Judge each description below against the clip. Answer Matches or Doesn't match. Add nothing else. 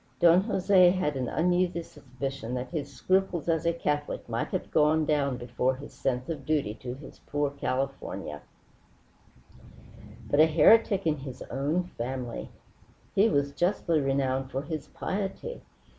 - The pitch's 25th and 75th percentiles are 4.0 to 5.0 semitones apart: Matches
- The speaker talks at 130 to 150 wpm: Matches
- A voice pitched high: Doesn't match